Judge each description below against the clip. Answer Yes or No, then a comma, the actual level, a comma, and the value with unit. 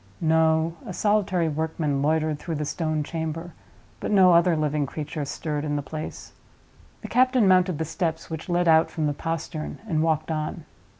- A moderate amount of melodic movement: No, narrow, 2.1 semitones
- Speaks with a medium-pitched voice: Yes, medium, 160 Hz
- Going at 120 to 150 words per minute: No, average, 175 wpm